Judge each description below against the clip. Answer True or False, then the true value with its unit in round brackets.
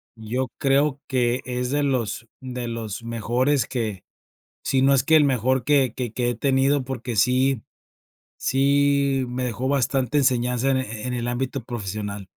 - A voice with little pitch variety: True (2.2 semitones)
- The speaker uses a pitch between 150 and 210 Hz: False (130 Hz)